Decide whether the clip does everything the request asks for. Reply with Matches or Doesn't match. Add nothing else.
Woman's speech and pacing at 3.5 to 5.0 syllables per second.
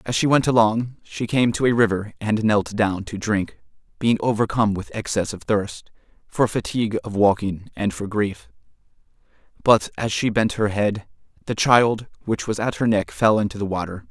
Doesn't match